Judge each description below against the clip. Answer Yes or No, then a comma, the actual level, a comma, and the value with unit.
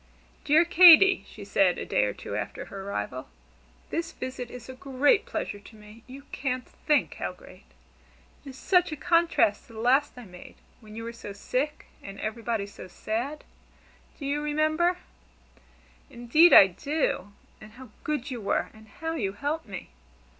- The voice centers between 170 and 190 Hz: No, very high, 250 Hz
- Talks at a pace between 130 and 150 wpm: No, average, 175 wpm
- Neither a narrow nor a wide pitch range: No, wide, 6.2 semitones